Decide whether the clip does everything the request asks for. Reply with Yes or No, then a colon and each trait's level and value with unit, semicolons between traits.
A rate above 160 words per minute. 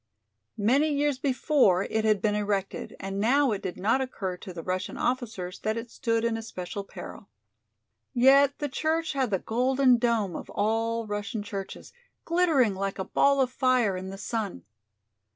Yes: average, 170 wpm